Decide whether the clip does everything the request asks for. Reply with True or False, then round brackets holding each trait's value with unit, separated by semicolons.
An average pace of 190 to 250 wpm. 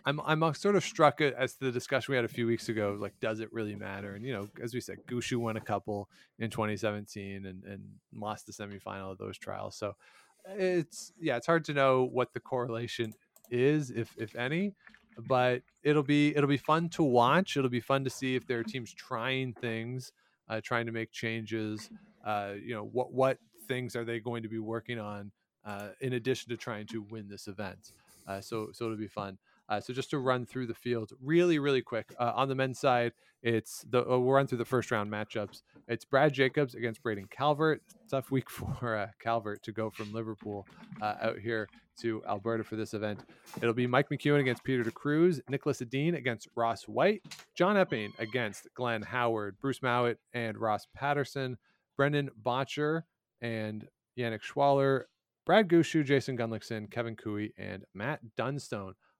True (195 wpm)